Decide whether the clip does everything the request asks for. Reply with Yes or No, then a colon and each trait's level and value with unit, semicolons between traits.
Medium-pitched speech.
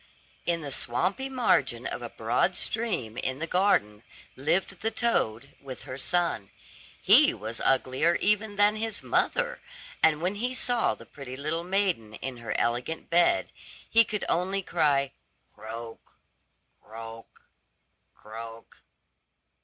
Yes: medium, 160 Hz